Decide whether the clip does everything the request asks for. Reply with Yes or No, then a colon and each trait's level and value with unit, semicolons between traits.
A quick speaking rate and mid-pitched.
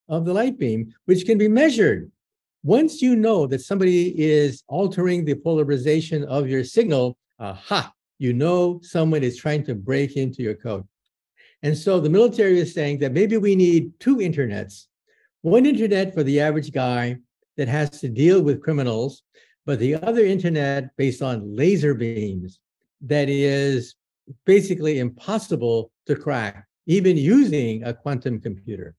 No: average, 155 wpm; medium, 145 Hz